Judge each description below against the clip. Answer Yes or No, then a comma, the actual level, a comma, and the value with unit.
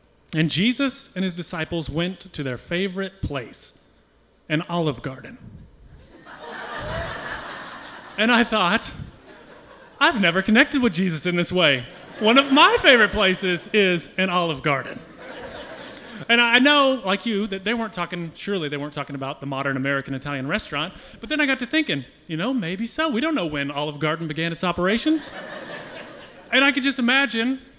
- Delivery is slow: No, average, 165 wpm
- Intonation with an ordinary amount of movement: No, wide, 7.4 semitones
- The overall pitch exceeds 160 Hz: Yes, medium, 185 Hz